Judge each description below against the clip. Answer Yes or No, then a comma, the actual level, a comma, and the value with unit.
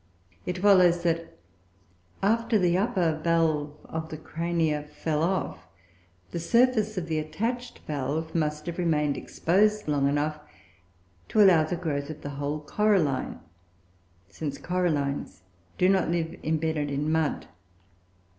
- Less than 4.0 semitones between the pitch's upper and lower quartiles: Yes, average, 3.3 semitones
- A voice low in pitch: No, medium, 160 Hz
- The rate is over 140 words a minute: No, slow, 135 wpm